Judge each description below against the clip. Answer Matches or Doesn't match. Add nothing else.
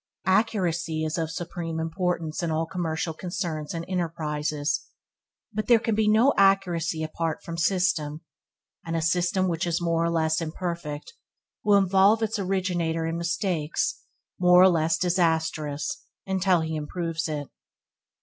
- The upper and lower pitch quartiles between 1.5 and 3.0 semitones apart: Matches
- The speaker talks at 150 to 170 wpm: Doesn't match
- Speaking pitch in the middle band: Matches